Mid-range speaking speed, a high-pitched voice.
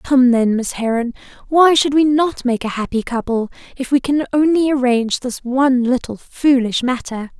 Yes: average, 180 wpm; very high, 255 Hz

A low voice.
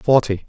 Yes: low, 115 Hz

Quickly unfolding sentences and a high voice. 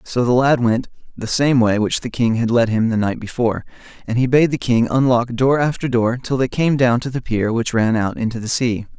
No: fast, 255 wpm; low, 120 Hz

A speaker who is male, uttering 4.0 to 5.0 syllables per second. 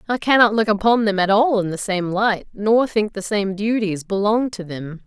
No: female; 4.8 syllables/s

